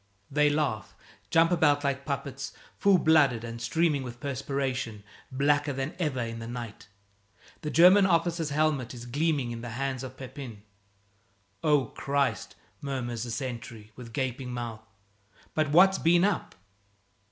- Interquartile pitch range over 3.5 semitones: Yes, average, 4.0 semitones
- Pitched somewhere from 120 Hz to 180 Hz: Yes, low, 135 Hz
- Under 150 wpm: Yes, average, 140 wpm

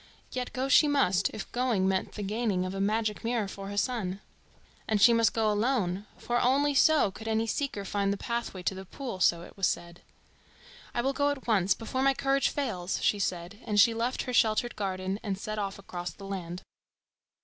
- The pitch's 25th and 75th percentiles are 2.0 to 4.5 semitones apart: Yes, average, 4.0 semitones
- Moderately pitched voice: No, high, 210 Hz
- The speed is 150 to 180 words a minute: No, fast, 205 wpm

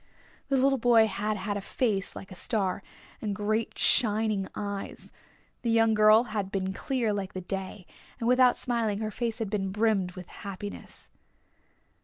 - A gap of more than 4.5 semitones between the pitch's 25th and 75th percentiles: No, average, 2.7 semitones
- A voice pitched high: Yes, high, 210 Hz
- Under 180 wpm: Yes, average, 165 wpm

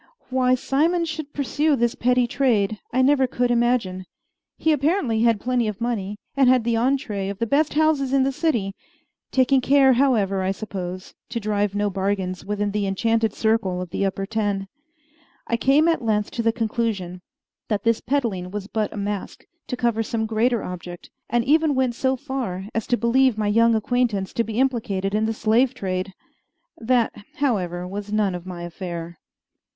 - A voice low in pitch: No, high, 225 Hz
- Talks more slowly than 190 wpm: Yes, average, 180 wpm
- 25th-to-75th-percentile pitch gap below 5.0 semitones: Yes, average, 4.5 semitones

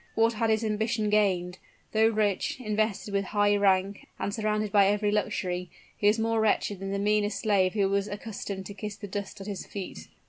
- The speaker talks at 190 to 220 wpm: Yes, average, 200 wpm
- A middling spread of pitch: No, narrow, 1.5 semitones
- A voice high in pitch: Yes, high, 205 Hz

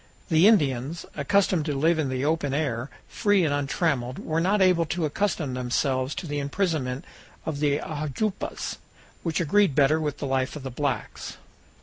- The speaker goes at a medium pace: Yes, average, 165 wpm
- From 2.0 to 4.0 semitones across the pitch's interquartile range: Yes, average, 3.7 semitones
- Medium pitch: Yes, medium, 150 Hz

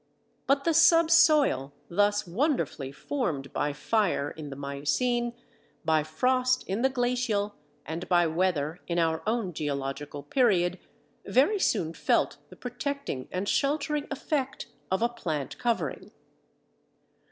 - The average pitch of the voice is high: Yes, high, 205 Hz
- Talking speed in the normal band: No, slow, 125 wpm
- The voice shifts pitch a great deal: Yes, wide, 8.7 semitones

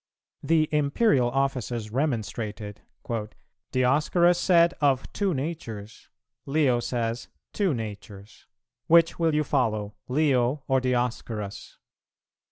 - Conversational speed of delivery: No, slow, 95 wpm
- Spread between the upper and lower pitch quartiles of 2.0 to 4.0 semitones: No, average, 5.3 semitones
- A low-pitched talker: Yes, low, 130 Hz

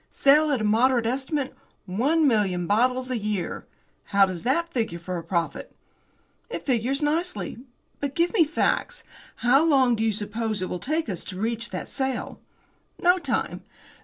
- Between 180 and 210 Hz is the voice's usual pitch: No, high, 245 Hz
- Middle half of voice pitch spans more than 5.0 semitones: Yes, wide, 5.5 semitones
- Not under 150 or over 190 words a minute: Yes, average, 165 wpm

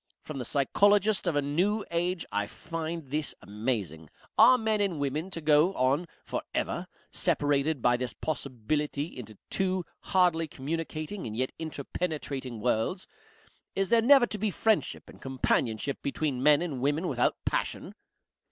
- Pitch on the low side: No, medium, 150 Hz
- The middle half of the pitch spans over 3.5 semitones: Yes, wide, 5.5 semitones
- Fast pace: No, average, 150 wpm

